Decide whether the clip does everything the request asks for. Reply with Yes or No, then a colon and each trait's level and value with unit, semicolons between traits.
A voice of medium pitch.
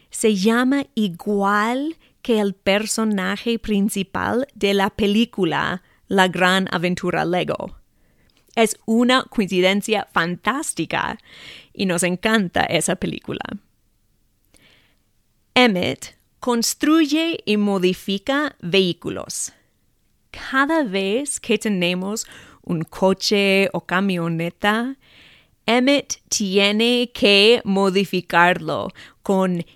No: high, 205 Hz